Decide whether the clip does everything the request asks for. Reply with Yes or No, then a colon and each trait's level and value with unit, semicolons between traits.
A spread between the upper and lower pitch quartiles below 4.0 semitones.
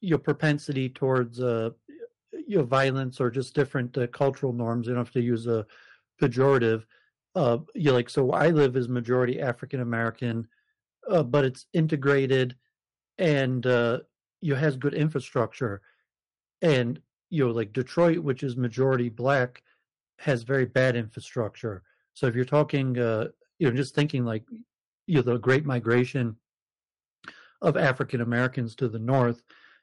Yes: average, 3.0 semitones